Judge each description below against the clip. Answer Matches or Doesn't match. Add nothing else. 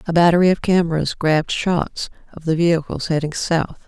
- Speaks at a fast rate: Doesn't match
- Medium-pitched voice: Matches